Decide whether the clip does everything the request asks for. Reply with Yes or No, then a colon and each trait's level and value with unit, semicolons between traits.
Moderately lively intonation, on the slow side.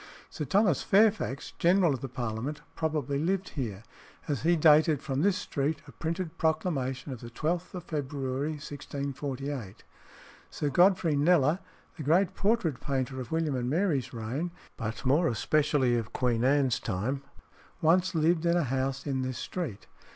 No: average, 4.2 semitones; average, 155 wpm